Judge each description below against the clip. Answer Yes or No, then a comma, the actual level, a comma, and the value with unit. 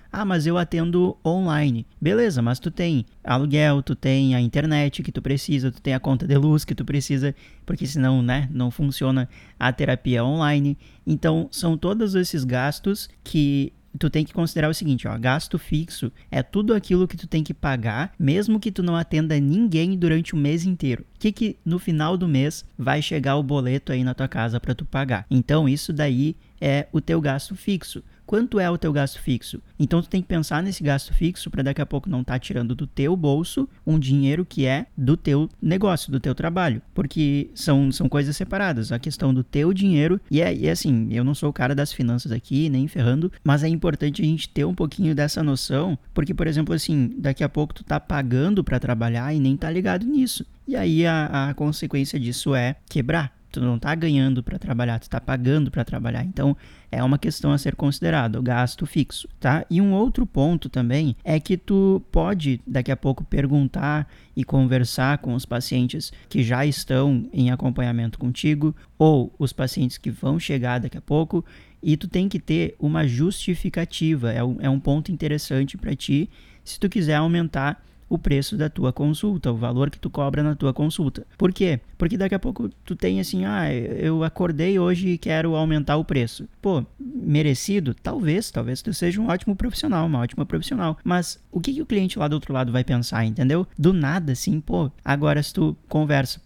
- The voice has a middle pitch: Yes, medium, 150 Hz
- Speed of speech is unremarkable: No, fast, 200 wpm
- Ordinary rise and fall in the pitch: Yes, average, 4.2 semitones